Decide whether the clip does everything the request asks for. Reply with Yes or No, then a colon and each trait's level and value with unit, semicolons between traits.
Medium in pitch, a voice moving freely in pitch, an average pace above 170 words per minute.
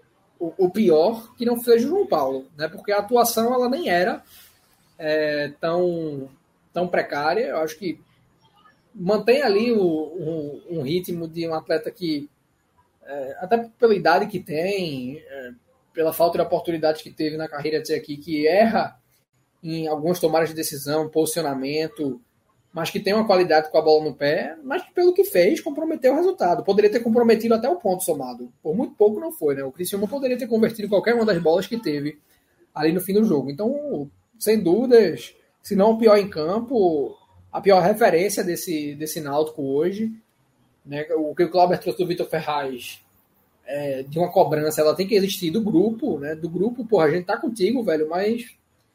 Yes: medium, 175 Hz; wide, 6.2 semitones; fast, 185 wpm